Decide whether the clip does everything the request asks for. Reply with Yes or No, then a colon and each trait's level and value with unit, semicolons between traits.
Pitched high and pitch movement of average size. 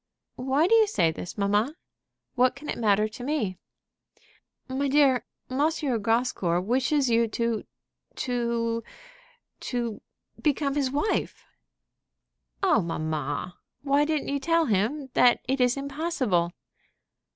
Yes: very high, 250 Hz; average, 5.0 semitones